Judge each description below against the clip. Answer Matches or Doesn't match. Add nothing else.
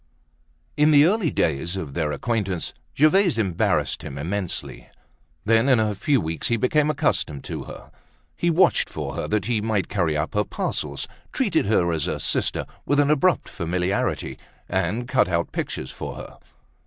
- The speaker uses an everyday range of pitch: Doesn't match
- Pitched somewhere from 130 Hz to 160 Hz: Doesn't match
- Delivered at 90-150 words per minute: Doesn't match